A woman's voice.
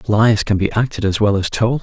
No: male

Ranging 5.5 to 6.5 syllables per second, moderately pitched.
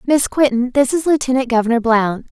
No: 5.6 syllables/s; very high, 255 Hz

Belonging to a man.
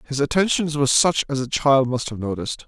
Yes: male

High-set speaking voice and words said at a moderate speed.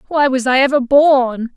Yes: very high, 265 Hz; average, 190 wpm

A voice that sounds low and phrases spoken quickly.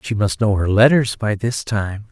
Yes: low, 105 Hz; fast, 225 wpm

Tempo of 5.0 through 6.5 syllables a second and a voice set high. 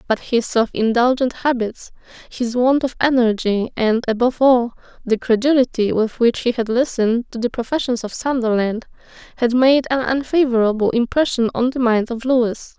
Yes: 5.1 syllables/s; high, 240 Hz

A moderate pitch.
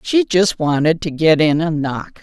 Yes: medium, 165 Hz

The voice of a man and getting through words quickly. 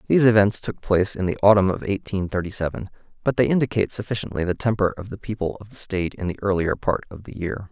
Yes: male; fast, 235 wpm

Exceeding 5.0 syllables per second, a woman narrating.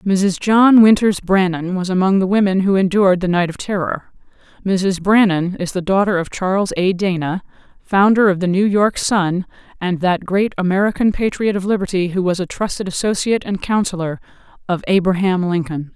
Yes: 5.2 syllables/s; female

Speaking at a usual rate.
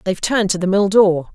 No: fast, 265 wpm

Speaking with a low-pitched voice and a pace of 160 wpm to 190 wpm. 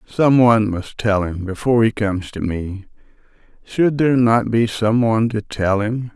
Yes: low, 110 Hz; average, 185 wpm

